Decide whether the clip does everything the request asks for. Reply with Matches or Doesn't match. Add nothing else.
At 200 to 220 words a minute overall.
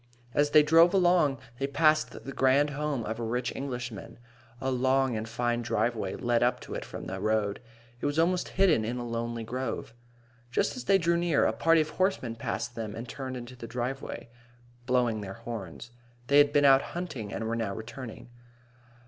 Doesn't match